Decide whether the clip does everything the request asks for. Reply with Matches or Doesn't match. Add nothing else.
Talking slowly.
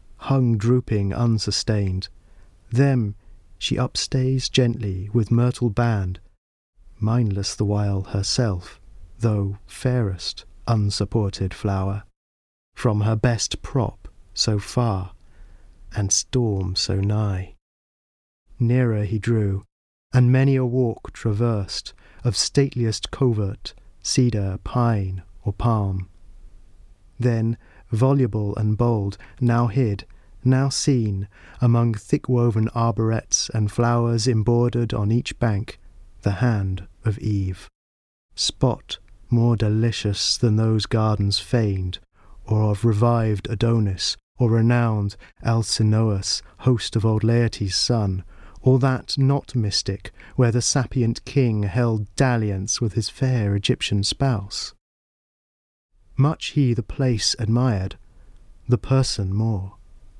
Matches